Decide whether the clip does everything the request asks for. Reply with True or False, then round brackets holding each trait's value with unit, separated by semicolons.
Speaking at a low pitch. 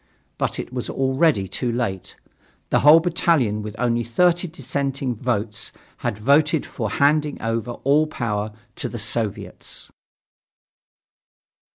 True (125 Hz)